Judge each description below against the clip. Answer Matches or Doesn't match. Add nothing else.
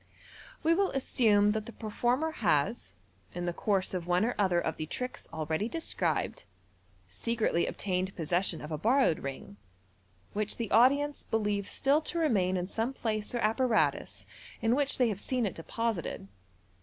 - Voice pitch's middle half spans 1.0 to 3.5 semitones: Doesn't match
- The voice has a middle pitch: Doesn't match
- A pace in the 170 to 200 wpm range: Doesn't match